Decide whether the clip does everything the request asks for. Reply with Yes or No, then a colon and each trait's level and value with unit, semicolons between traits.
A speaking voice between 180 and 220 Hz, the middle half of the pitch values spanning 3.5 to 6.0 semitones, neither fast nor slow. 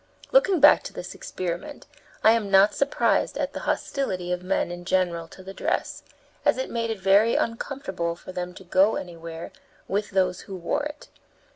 Yes: high, 190 Hz; average, 4.4 semitones; average, 180 wpm